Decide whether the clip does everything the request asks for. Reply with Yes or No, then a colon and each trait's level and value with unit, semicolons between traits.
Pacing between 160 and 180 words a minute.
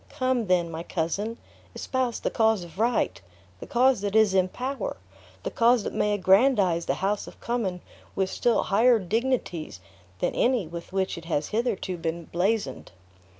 Yes: average, 165 wpm